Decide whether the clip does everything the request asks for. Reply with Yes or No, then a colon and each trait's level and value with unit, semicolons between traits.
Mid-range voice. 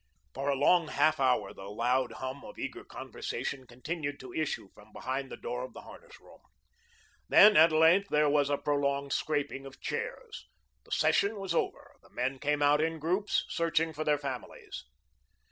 Yes: medium, 145 Hz